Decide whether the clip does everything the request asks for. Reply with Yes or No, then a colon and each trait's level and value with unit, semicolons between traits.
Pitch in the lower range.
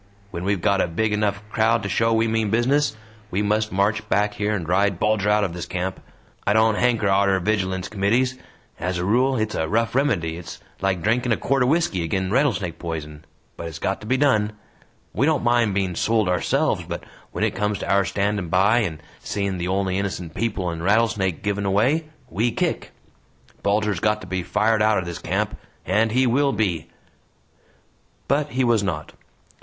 Yes: low, 105 Hz